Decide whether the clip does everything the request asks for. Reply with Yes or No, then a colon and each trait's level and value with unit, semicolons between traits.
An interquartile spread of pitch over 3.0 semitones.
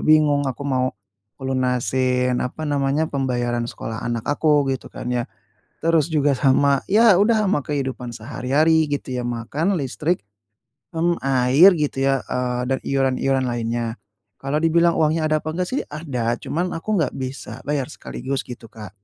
Yes: average, 3.7 semitones